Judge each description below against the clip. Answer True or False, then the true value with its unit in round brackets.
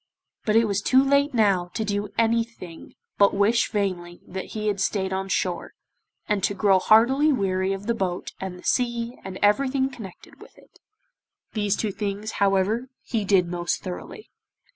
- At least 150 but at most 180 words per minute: True (170 wpm)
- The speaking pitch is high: True (205 Hz)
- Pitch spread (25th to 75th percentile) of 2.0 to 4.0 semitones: True (3.4 semitones)